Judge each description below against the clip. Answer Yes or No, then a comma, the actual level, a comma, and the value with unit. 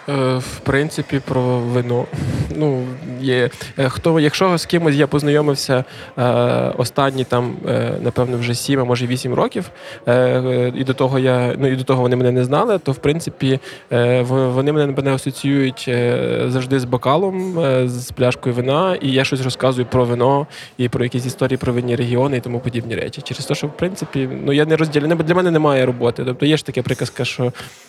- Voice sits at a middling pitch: No, low, 130 Hz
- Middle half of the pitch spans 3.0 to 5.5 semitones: No, narrow, 2.4 semitones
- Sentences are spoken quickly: Yes, fast, 175 wpm